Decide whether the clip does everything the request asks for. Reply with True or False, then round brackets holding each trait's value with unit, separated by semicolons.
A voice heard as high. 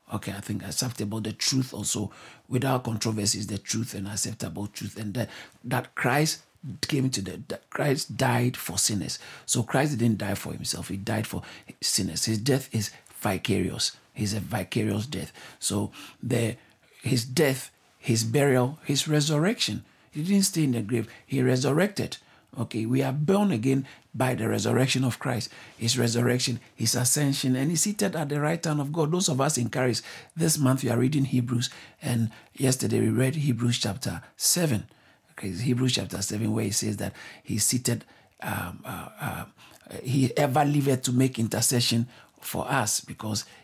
False (125 Hz)